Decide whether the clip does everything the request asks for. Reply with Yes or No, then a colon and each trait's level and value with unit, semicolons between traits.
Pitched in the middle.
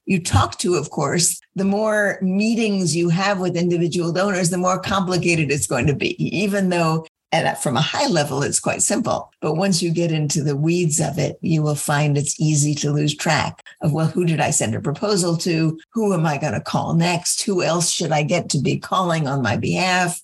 Yes: medium, 170 Hz